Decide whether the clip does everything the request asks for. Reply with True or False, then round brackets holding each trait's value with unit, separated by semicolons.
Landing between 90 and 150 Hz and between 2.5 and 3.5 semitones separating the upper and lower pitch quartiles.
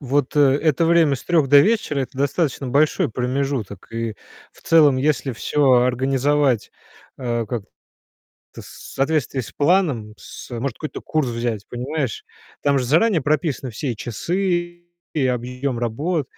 False (140 Hz; 4.0 semitones)